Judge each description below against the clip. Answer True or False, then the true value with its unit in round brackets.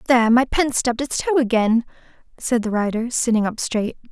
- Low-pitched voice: False (235 Hz)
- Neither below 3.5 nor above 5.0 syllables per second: False (5.5 syllables/s)